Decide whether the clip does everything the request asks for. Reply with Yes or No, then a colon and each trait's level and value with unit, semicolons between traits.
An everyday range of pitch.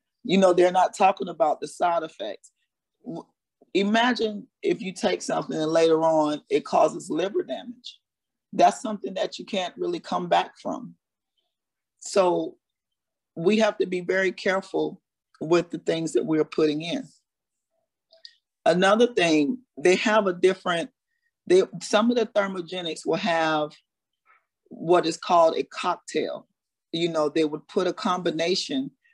No: wide, 6.7 semitones